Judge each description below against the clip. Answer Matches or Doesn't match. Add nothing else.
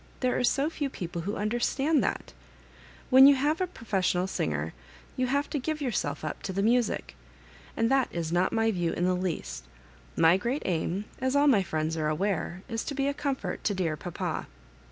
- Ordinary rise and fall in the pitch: Doesn't match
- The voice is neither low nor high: Doesn't match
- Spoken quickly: Doesn't match